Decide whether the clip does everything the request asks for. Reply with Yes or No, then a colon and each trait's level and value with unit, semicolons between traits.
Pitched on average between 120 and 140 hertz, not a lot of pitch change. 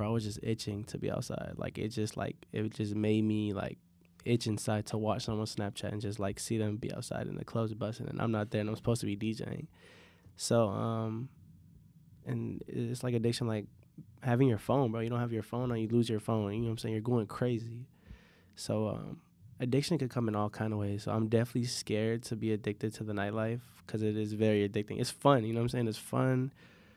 No: low, 110 Hz; narrow, 2.2 semitones